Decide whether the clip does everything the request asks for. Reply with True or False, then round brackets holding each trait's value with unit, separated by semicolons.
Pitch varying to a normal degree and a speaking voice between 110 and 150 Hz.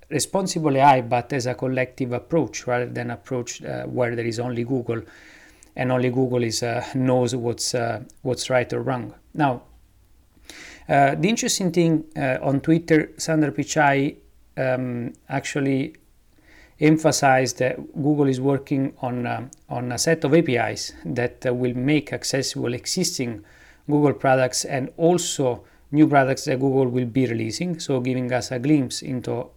True (3.1 semitones; 130 Hz)